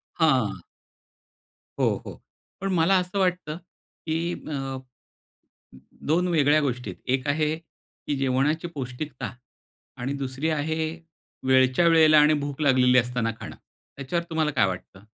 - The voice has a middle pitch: Yes, medium, 145 Hz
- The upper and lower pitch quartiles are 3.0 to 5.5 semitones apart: Yes, average, 3.6 semitones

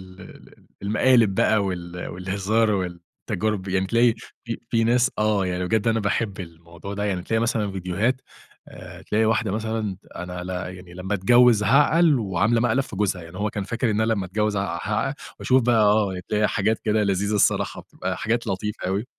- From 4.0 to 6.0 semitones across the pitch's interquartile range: No, average, 3.2 semitones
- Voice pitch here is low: Yes, low, 105 Hz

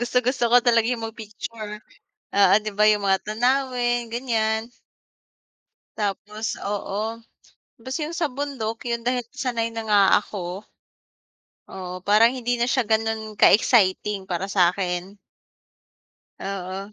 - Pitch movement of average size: Yes, average, 3.2 semitones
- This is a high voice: Yes, high, 220 Hz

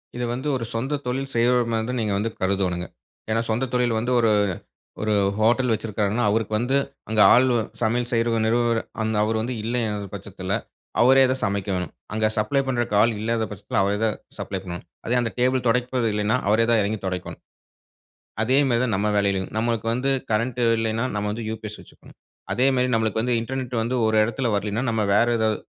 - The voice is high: No, low, 115 Hz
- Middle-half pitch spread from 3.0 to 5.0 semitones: No, narrow, 2.4 semitones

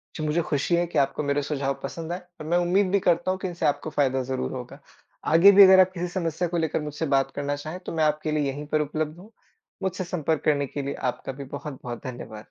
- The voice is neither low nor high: Yes, medium, 155 Hz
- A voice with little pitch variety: No, average, 3.6 semitones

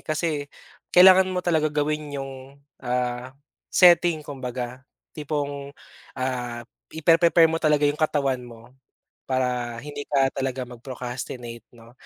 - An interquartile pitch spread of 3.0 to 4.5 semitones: Yes, average, 3.7 semitones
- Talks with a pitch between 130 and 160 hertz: Yes, low, 135 Hz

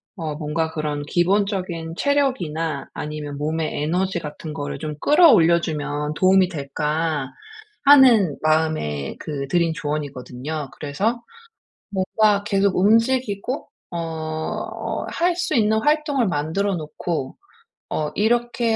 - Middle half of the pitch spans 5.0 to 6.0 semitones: Yes, wide, 5.5 semitones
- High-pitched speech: No, medium, 165 Hz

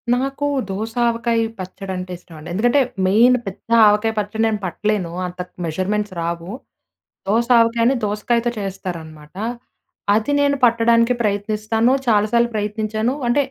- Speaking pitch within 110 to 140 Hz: No, high, 215 Hz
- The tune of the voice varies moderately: Yes, average, 3.5 semitones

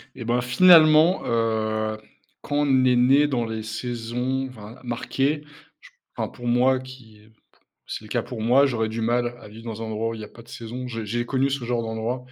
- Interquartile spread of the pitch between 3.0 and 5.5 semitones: No, narrow, 2.5 semitones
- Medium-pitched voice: No, low, 120 Hz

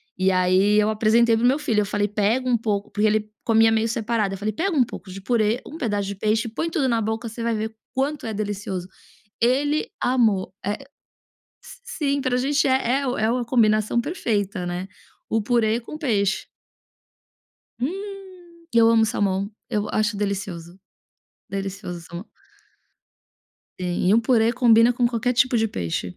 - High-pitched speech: Yes, high, 220 Hz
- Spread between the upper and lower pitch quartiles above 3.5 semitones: No, average, 3.2 semitones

